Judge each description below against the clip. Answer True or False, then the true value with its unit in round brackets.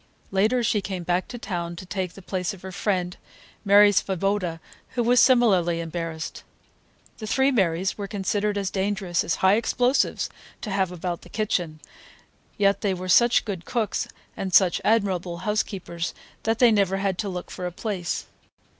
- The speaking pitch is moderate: False (195 Hz)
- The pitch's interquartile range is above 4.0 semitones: False (2.9 semitones)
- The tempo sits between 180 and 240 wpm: False (170 wpm)